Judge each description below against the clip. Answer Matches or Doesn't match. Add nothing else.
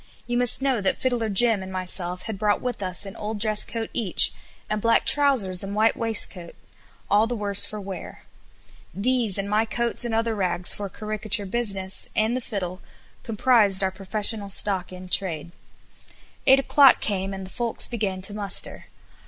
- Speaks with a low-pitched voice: Doesn't match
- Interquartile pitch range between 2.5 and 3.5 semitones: Matches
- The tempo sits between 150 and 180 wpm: Matches